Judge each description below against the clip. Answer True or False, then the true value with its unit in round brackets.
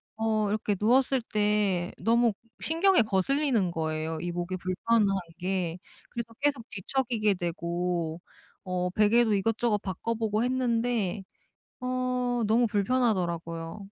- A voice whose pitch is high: True (210 Hz)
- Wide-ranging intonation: False (4.9 semitones)